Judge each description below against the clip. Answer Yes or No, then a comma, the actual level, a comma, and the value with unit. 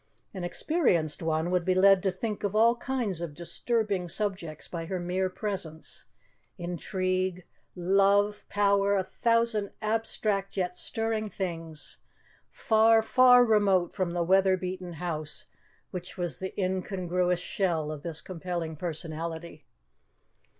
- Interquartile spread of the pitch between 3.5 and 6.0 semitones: No, average, 3.0 semitones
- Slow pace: Yes, slow, 130 wpm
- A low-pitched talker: No, medium, 185 Hz